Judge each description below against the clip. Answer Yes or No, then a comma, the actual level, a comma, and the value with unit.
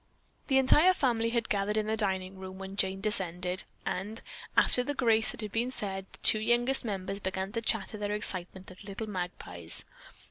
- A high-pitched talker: Yes, high, 205 Hz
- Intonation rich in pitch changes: No, average, 3.2 semitones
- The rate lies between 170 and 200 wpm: Yes, average, 180 wpm